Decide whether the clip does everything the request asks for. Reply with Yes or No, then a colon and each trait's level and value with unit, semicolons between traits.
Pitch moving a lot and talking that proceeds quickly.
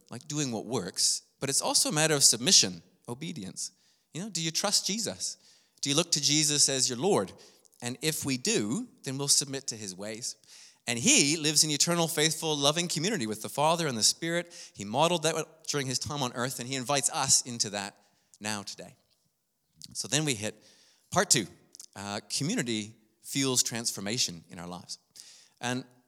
No: wide, 5.9 semitones; average, 185 wpm